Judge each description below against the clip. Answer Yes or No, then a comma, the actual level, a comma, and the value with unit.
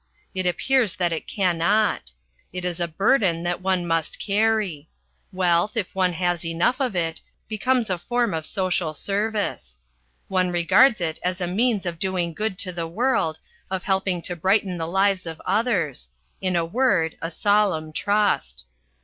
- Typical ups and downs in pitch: Yes, average, 3.5 semitones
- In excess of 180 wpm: No, average, 165 wpm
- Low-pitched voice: No, medium, 185 Hz